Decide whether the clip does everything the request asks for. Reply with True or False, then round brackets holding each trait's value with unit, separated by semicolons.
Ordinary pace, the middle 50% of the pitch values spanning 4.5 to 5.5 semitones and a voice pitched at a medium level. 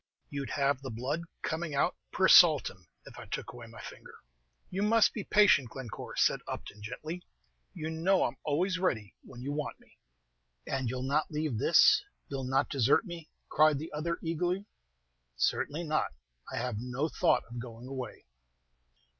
True (165 wpm; 4.9 semitones; 145 Hz)